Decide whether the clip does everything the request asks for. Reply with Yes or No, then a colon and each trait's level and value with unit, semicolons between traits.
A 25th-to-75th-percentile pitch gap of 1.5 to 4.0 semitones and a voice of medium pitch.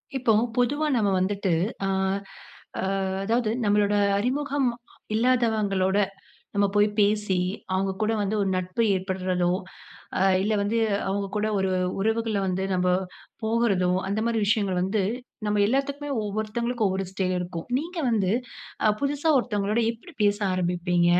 No: average, 3.5 semitones; high, 205 Hz